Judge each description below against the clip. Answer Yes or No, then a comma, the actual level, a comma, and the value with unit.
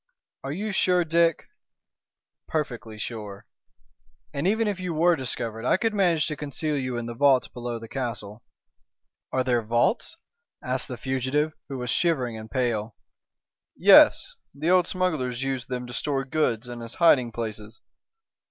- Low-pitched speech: Yes, low, 130 Hz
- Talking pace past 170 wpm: No, average, 155 wpm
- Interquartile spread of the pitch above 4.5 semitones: Yes, average, 5.1 semitones